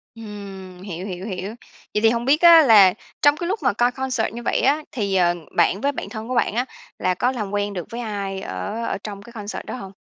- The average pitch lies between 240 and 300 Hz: No, high, 210 Hz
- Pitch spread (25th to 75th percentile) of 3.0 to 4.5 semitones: Yes, average, 4.0 semitones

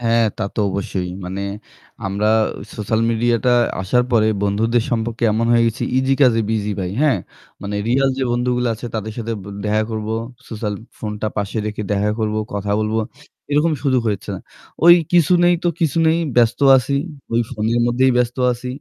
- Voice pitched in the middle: No, low, 115 Hz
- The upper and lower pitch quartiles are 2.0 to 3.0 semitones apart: Yes, narrow, 2.5 semitones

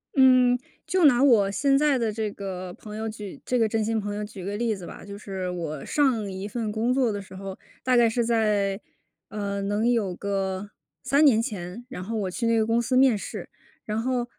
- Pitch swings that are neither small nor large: Yes, average, 3.5 semitones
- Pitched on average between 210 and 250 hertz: Yes, high, 220 Hz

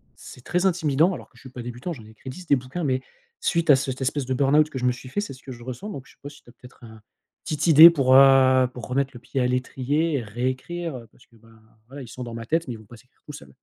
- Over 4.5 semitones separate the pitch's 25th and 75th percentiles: No, average, 3.3 semitones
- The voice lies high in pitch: No, low, 130 Hz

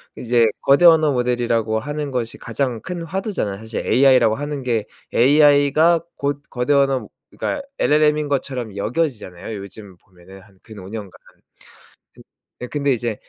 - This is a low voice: Yes, low, 125 Hz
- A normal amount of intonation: Yes, average, 4.9 semitones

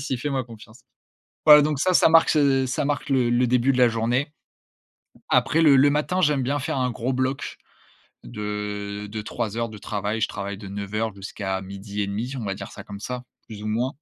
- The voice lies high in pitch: No, low, 120 Hz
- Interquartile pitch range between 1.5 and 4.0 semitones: No, average, 4.6 semitones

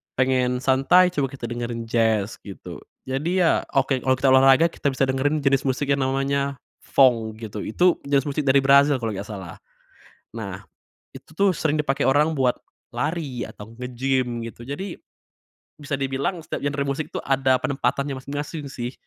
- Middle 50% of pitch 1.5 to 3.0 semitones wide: Yes, narrow, 2.4 semitones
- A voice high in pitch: No, low, 135 Hz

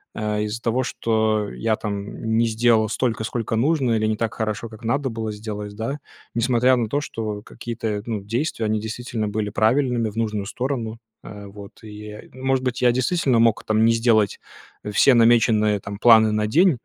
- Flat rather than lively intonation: Yes, narrow, 2.1 semitones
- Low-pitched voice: Yes, low, 110 Hz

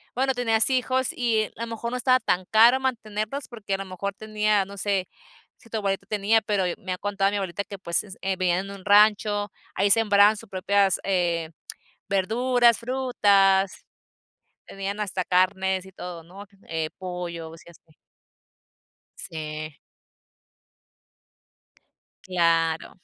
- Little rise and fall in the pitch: No, average, 3.0 semitones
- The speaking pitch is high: Yes, high, 200 Hz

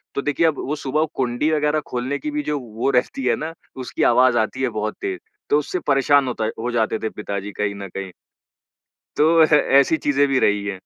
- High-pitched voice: No, low, 135 Hz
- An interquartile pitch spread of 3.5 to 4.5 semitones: No, average, 5.0 semitones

